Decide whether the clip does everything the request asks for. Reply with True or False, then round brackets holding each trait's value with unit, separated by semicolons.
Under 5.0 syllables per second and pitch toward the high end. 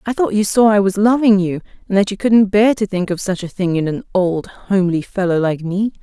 False (5.4 syllables/s; 195 Hz)